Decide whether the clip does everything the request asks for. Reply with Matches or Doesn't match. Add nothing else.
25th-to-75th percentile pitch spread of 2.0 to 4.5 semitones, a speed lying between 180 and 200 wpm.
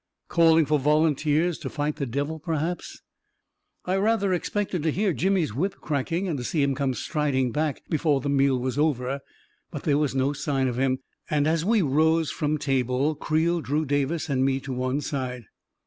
Matches